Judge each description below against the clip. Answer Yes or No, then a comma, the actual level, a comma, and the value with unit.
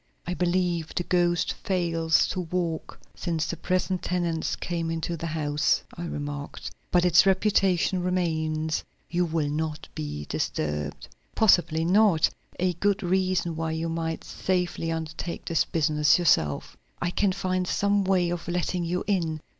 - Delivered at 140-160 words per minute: Yes, average, 145 wpm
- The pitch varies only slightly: Yes, narrow, 2.2 semitones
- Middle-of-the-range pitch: Yes, medium, 170 Hz